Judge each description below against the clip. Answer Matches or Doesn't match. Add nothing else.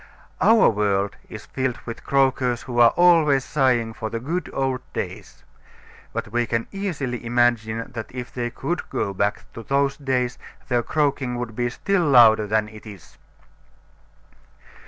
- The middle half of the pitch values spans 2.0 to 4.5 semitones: Matches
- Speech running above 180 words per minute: Doesn't match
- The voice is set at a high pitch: Doesn't match